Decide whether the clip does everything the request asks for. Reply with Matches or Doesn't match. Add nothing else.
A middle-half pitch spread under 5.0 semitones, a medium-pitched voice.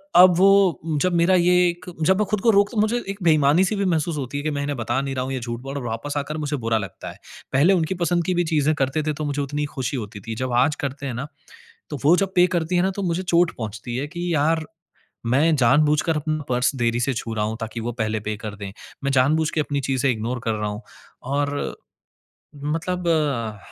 Doesn't match